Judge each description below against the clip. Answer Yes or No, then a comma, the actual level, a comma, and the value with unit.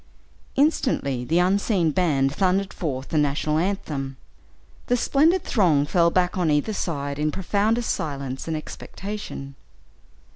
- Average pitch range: No, wide, 5.7 semitones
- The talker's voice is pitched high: No, medium, 165 Hz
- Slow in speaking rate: Yes, slow, 130 wpm